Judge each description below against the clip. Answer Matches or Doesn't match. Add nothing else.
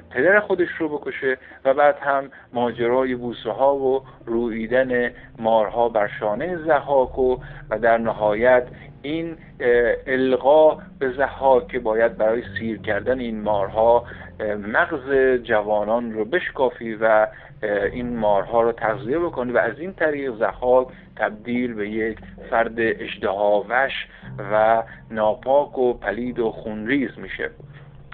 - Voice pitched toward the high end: Doesn't match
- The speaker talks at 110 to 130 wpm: Matches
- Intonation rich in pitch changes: Doesn't match